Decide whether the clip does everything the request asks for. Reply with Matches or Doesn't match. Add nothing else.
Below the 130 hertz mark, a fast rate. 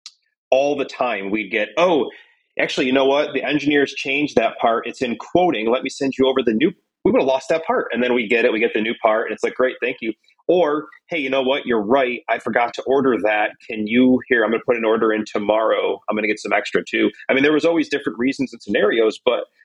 Doesn't match